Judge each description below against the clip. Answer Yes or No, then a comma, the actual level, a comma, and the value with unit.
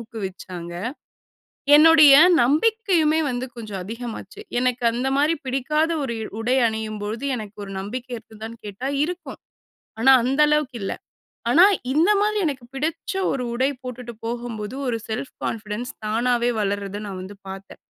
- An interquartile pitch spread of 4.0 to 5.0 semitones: Yes, average, 4.5 semitones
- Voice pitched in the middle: No, high, 245 Hz